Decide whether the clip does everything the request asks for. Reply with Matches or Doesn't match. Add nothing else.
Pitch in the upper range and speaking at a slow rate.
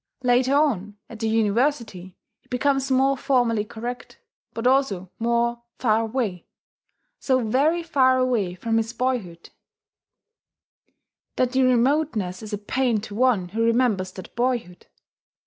Matches